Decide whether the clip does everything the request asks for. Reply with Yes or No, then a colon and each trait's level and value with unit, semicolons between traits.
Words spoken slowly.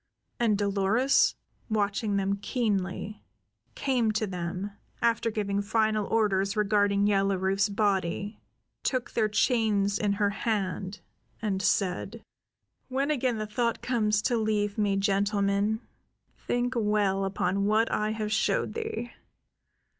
Yes: slow, 125 wpm